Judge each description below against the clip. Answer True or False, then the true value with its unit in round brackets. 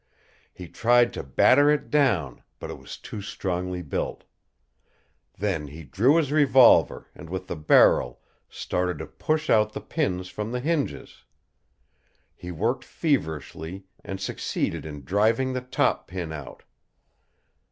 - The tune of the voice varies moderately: False (7.7 semitones)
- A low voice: True (95 Hz)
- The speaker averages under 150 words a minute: True (140 wpm)